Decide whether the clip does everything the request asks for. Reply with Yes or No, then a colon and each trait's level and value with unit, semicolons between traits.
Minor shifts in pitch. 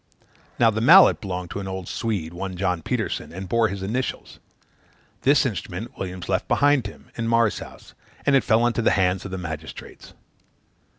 No: average, 4.2 semitones